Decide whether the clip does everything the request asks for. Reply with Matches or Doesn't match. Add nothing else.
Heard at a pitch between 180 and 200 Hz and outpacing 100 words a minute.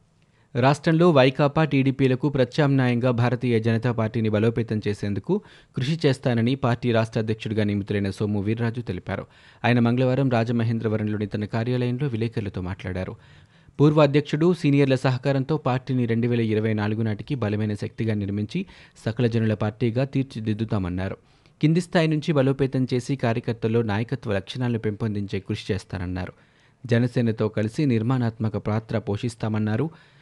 Doesn't match